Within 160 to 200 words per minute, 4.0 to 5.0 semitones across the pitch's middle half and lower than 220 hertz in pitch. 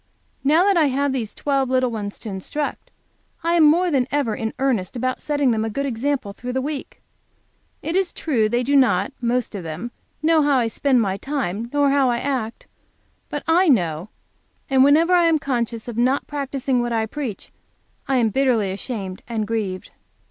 No: average, 190 wpm; average, 4.3 semitones; very high, 255 Hz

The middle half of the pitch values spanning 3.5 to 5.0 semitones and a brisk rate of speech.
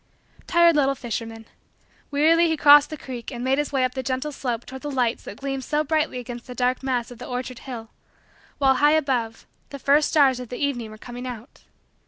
No: average, 2.9 semitones; fast, 215 wpm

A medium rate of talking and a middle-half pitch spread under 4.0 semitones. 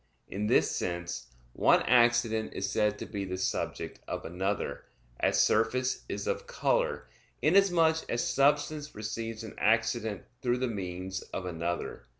No: average, 145 wpm; average, 5.0 semitones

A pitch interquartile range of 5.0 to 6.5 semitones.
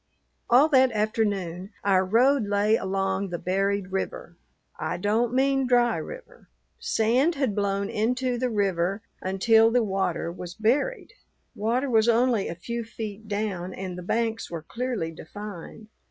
No: average, 3.9 semitones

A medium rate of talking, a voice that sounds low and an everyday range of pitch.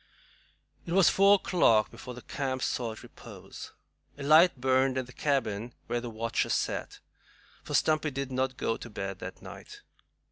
Yes: average, 165 wpm; low, 130 Hz; average, 3.5 semitones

